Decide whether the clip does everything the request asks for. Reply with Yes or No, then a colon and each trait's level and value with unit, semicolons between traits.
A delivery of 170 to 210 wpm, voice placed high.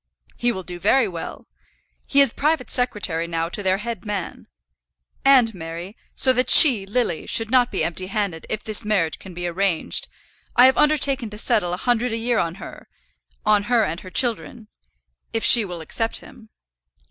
Yes: average, 180 wpm; high, 215 Hz